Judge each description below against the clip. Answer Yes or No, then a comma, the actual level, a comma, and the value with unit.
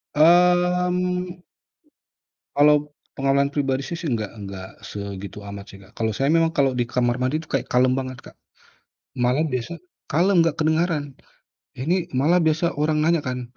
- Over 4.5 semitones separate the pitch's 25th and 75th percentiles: Yes, average, 5.2 semitones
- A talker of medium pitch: Yes, medium, 145 Hz